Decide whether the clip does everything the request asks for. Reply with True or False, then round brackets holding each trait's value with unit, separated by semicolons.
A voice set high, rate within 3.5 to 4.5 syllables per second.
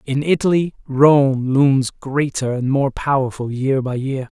False (135 Hz; 3.9 syllables/s)